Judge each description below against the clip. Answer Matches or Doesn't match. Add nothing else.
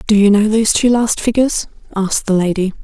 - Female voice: Matches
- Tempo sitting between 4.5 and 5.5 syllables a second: Doesn't match